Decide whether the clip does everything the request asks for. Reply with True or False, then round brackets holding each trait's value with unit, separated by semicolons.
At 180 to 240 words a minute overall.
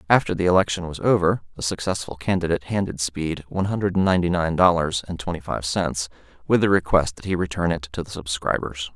True (195 wpm)